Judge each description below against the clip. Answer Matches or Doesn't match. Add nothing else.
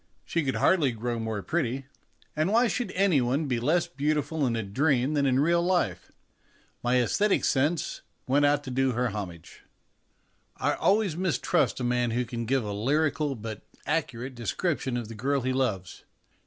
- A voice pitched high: Doesn't match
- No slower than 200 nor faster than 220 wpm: Doesn't match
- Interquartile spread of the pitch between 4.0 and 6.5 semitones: Matches